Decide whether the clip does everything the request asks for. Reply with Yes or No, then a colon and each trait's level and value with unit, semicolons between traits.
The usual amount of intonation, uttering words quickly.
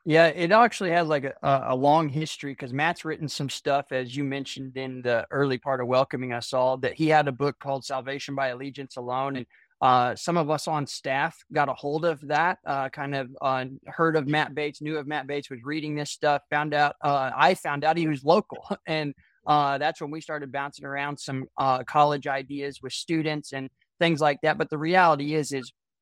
No: narrow, 2.3 semitones; fast, 220 wpm